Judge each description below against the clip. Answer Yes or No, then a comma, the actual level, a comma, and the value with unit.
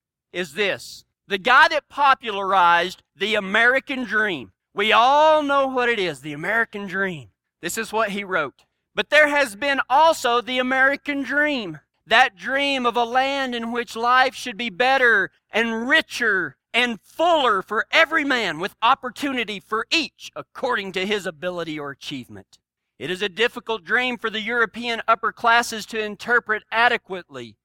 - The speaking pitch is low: No, high, 230 Hz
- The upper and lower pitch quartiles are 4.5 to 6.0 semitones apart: Yes, average, 4.8 semitones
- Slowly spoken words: No, average, 155 wpm